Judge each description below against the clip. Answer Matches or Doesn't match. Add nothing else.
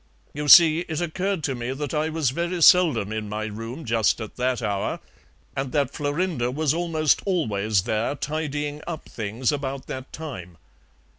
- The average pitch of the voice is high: Doesn't match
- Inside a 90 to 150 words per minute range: Doesn't match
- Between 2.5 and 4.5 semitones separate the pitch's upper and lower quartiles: Doesn't match